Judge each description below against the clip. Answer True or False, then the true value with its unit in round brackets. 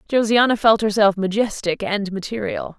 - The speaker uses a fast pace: False (130 wpm)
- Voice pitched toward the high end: True (210 Hz)